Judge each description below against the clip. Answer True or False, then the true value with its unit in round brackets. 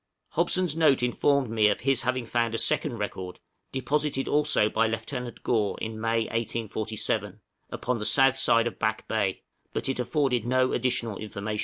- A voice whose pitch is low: True (120 Hz)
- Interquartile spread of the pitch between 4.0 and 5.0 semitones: False (3.3 semitones)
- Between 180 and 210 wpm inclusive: False (165 wpm)